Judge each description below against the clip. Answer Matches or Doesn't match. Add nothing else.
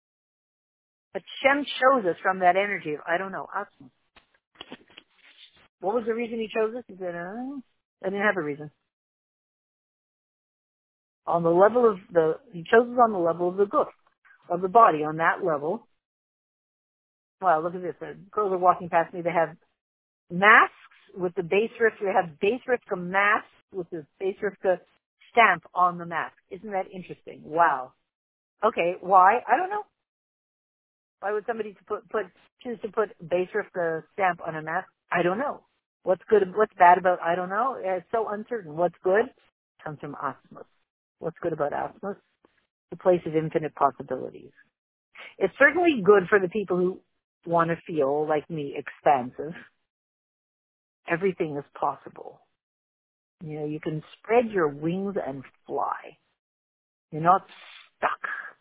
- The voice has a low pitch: Doesn't match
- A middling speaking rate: Matches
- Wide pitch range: Doesn't match